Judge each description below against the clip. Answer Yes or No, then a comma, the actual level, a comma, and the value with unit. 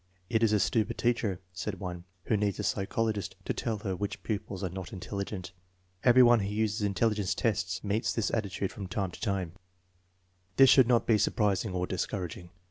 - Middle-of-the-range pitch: No, low, 100 Hz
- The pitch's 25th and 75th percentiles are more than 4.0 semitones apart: No, average, 2.8 semitones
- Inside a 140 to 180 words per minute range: No, average, 200 wpm